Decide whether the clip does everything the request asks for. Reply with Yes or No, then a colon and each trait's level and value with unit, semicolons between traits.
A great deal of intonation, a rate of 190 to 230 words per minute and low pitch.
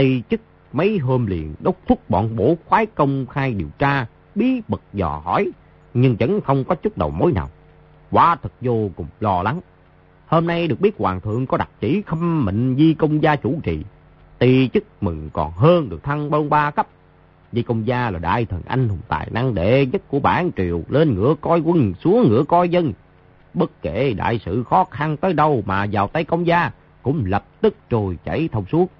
Yes: wide, 8.7 semitones; average, 210 wpm; low, 130 Hz